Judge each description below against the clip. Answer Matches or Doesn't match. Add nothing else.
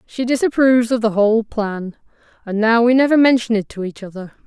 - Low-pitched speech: Doesn't match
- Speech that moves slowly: Doesn't match